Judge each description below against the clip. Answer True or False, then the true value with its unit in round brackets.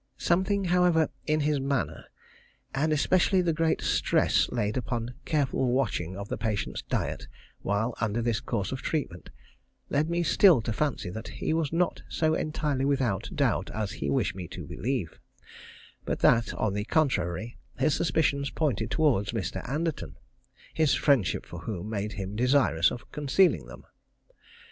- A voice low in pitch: True (130 Hz)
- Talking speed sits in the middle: True (155 wpm)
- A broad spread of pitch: True (6.6 semitones)